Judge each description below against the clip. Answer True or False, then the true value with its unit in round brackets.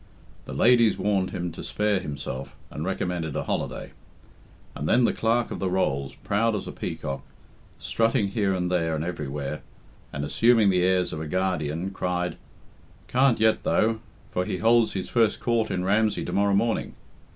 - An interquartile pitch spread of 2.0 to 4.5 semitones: False (5.1 semitones)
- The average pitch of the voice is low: True (95 Hz)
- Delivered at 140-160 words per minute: False (170 wpm)